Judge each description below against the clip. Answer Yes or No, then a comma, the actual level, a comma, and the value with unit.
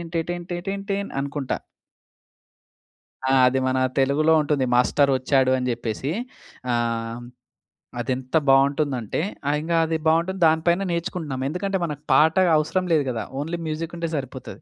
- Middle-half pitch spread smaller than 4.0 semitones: No, average, 4.3 semitones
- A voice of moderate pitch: Yes, medium, 150 Hz